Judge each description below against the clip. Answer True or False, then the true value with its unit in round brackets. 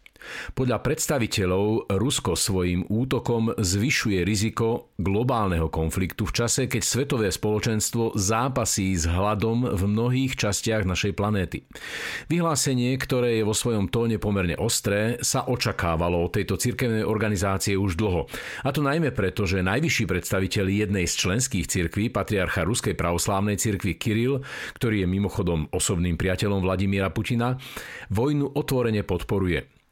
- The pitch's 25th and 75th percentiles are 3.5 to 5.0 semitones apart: True (3.8 semitones)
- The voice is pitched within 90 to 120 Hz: True (105 Hz)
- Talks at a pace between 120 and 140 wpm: True (130 wpm)